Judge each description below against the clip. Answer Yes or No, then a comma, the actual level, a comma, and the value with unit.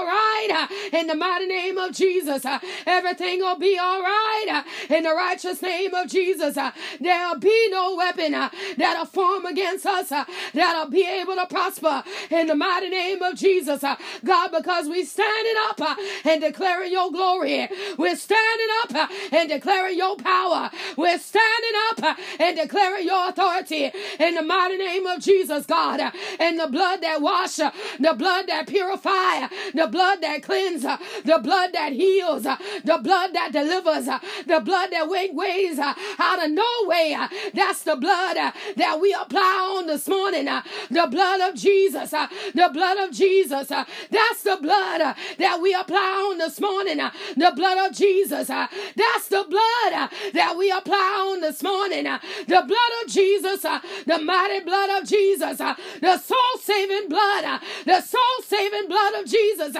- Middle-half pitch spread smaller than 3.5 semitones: Yes, average, 2.9 semitones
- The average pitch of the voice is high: Yes, very high, 370 Hz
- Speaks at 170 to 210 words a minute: No, average, 155 wpm